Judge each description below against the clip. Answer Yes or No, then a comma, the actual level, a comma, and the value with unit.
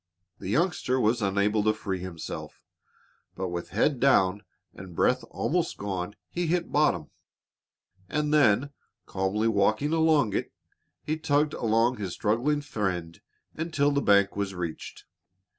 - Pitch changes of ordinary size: No, wide, 7.1 semitones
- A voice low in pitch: Yes, low, 110 Hz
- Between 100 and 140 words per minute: Yes, slow, 135 wpm